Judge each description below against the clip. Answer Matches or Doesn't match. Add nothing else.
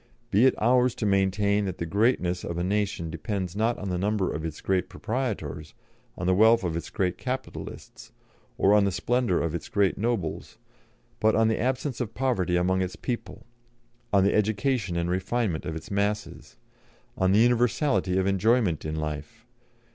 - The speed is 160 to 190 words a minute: Matches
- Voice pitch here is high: Doesn't match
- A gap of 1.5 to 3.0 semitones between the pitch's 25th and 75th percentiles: Doesn't match